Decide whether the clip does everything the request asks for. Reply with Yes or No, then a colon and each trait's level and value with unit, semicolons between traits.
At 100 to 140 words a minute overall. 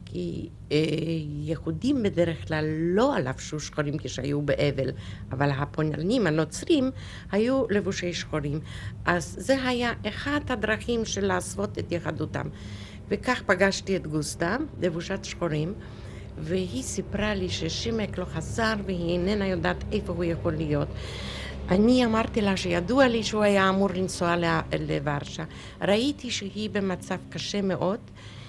Yes: average, 125 wpm